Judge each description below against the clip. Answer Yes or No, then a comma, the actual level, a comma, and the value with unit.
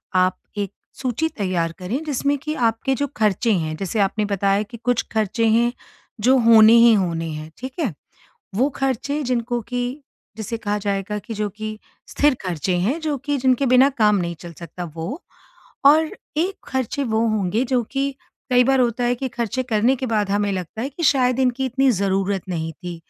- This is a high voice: Yes, high, 225 Hz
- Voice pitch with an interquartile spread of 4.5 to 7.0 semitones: Yes, average, 4.8 semitones